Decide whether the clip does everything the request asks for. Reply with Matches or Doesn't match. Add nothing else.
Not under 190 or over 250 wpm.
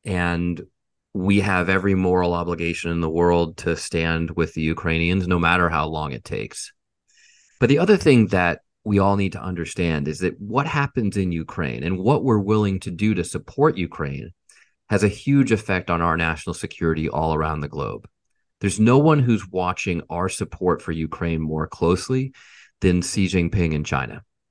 Doesn't match